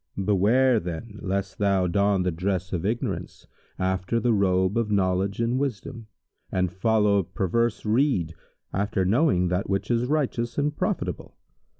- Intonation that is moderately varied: Yes, average, 3.9 semitones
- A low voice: Yes, low, 100 Hz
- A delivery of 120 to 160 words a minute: Yes, average, 140 wpm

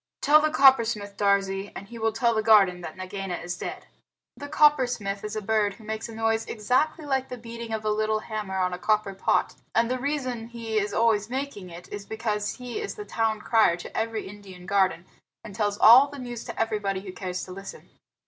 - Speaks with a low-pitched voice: No, high, 215 Hz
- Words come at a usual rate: No, fast, 215 wpm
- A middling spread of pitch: Yes, average, 3.0 semitones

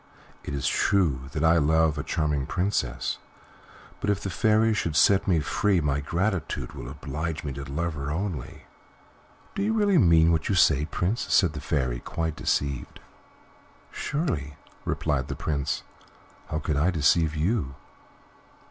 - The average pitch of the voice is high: No, very low, 80 Hz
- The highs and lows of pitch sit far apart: No, average, 4.6 semitones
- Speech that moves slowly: No, average, 155 wpm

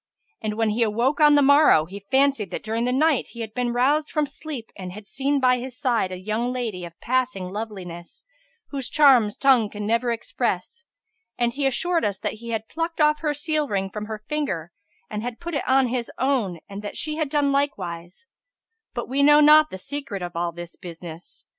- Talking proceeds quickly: Yes, fast, 210 wpm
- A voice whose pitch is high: Yes, high, 240 Hz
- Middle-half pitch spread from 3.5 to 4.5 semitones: No, wide, 5.6 semitones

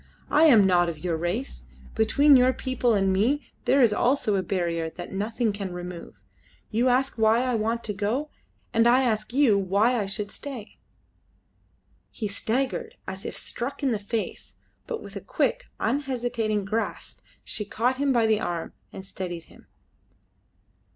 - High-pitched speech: Yes, high, 220 Hz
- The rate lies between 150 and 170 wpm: Yes, average, 165 wpm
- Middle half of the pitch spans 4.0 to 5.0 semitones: Yes, average, 4.5 semitones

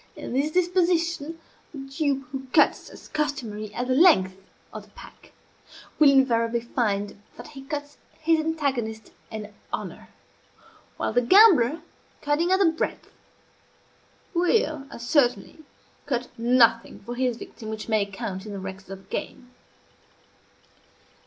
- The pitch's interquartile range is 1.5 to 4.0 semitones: No, wide, 5.5 semitones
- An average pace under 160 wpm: Yes, average, 140 wpm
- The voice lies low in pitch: No, very high, 255 Hz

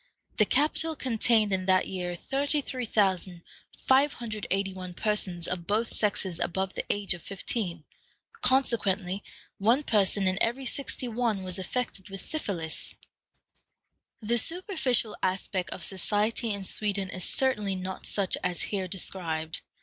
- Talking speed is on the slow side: Yes, slow, 125 wpm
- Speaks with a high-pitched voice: Yes, high, 200 Hz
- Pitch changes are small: No, average, 4.0 semitones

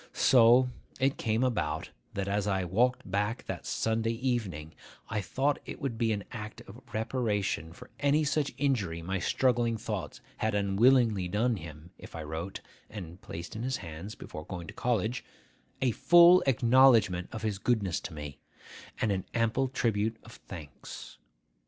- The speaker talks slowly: No, average, 160 wpm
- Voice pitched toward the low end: Yes, low, 110 Hz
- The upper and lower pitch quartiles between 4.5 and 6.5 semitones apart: Yes, average, 4.8 semitones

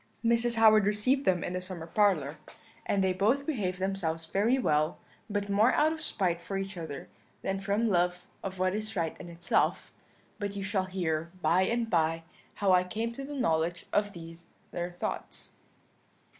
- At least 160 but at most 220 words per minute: Yes, average, 180 wpm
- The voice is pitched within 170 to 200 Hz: Yes, high, 190 Hz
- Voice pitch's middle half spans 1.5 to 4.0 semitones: Yes, average, 3.7 semitones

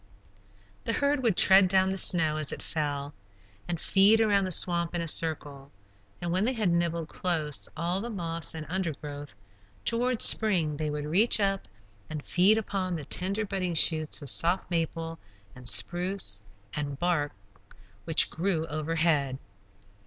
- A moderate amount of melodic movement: Yes, average, 3.9 semitones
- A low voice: No, medium, 170 Hz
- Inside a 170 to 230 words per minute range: No, average, 155 wpm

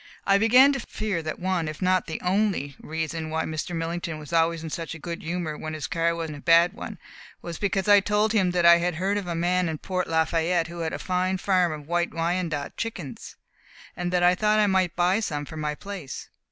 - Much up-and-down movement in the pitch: No, average, 2.7 semitones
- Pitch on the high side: No, medium, 175 Hz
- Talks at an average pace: No, fast, 235 wpm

